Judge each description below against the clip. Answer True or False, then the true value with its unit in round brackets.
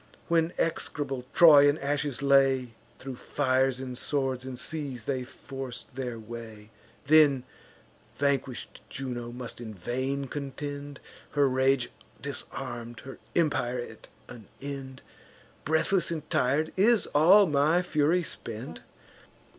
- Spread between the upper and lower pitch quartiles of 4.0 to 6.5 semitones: False (2.7 semitones)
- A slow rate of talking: True (120 wpm)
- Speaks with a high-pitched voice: False (135 Hz)